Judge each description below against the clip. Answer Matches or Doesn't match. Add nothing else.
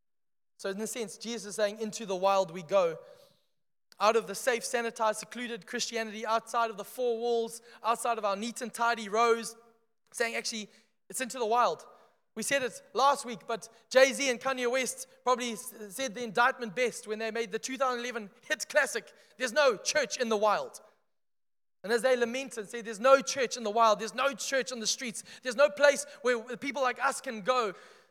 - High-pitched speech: Matches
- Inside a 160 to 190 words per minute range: Doesn't match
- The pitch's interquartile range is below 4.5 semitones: Matches